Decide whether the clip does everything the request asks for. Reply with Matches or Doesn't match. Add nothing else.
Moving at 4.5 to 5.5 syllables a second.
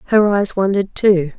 Matches